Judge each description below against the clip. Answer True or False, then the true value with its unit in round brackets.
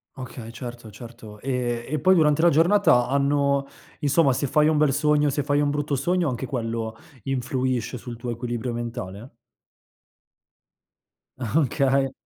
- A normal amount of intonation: True (3.5 semitones)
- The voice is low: True (130 Hz)